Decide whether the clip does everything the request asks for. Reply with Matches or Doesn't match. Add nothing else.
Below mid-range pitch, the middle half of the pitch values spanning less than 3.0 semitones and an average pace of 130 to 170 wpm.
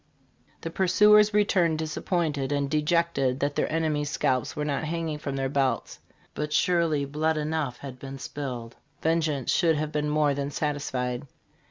Doesn't match